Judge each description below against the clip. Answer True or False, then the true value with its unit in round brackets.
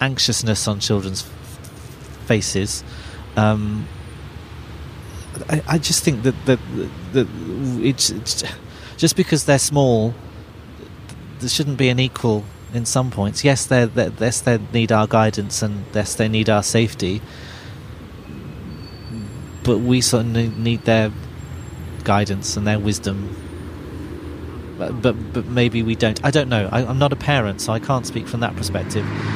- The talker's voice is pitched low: True (110 Hz)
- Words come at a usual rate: True (145 wpm)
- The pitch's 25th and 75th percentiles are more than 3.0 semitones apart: True (3.5 semitones)